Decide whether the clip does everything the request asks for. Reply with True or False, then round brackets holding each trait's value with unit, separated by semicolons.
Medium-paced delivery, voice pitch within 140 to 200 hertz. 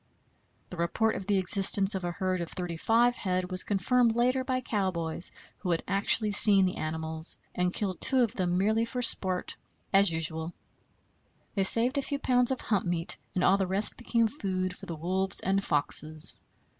True (185 wpm; 190 Hz)